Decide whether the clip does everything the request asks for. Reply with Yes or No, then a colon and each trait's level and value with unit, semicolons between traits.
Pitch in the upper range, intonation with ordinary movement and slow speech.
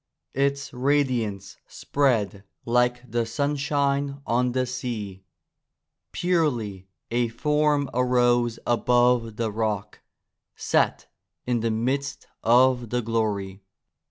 No: low, 120 Hz; average, 3.5 semitones; slow, 100 wpm